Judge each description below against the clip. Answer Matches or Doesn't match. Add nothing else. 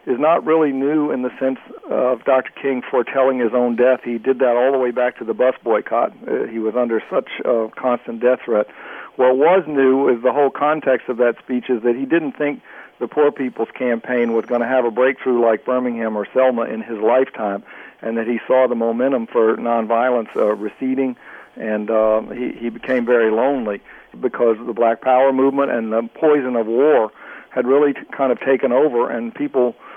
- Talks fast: Matches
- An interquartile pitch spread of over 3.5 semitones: Doesn't match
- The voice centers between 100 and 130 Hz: Matches